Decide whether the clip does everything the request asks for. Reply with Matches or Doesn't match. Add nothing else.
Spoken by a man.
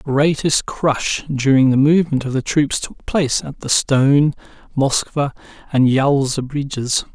Matches